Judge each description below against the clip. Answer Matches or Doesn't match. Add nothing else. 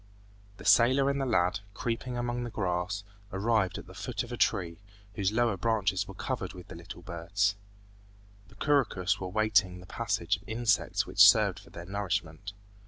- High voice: Doesn't match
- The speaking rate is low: Doesn't match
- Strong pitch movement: Doesn't match